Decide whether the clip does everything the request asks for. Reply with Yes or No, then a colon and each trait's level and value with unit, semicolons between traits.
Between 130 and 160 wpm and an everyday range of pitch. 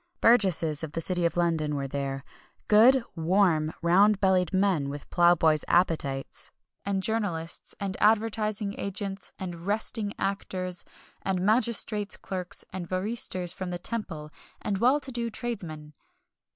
Yes: average, 140 wpm; average, 4.0 semitones